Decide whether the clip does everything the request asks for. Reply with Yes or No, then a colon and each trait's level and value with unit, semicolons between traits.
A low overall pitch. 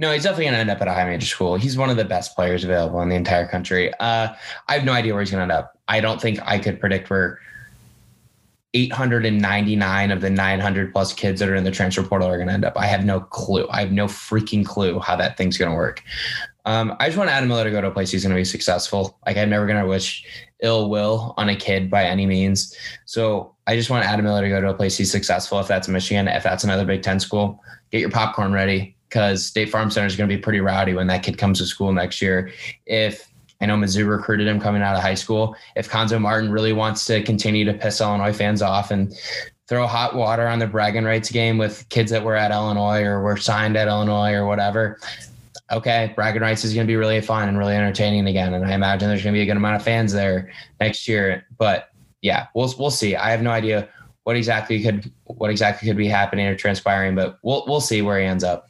Yes: low, 105 Hz